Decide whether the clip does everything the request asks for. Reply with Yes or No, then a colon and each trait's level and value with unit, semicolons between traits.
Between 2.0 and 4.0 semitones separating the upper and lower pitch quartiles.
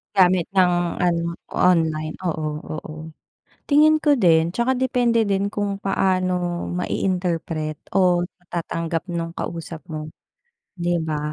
Yes: average, 2.9 semitones